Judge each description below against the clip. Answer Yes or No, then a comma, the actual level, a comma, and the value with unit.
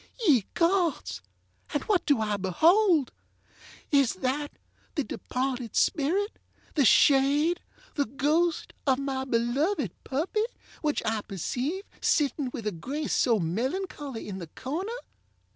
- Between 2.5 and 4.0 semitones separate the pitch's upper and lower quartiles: No, wide, 5.4 semitones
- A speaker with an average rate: No, slow, 120 wpm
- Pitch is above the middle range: Yes, very high, 275 Hz